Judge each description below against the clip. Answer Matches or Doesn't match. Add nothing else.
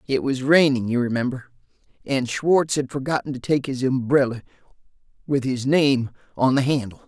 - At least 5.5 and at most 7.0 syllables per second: Doesn't match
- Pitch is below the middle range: Matches